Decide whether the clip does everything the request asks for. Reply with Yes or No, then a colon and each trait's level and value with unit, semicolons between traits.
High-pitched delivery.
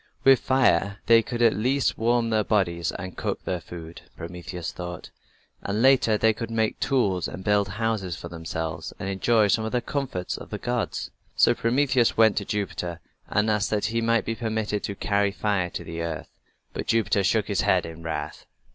No: low, 105 Hz